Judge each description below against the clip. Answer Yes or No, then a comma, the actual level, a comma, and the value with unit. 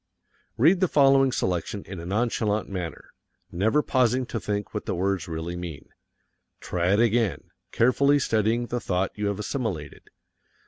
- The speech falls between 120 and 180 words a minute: Yes, average, 150 wpm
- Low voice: Yes, low, 105 Hz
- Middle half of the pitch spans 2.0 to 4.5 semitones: No, average, 5.2 semitones